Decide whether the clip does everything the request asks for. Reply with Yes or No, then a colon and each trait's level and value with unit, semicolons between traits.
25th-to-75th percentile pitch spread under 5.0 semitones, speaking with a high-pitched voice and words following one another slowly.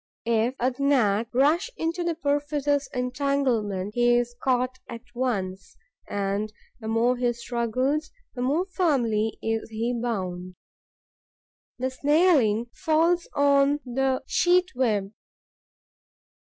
Yes: average, 4.2 semitones; very high, 250 Hz; slow, 110 wpm